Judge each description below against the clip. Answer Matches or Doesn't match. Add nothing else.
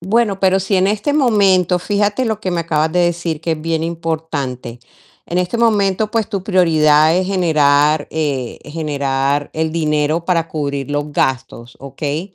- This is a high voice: Doesn't match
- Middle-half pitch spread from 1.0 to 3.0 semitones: Doesn't match